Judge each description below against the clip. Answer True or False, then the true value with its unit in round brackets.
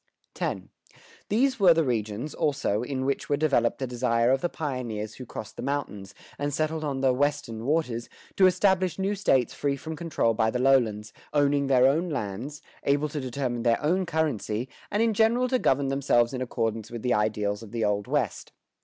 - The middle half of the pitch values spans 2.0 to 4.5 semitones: False (4.9 semitones)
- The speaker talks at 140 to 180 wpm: False (195 wpm)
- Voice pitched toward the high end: False (135 Hz)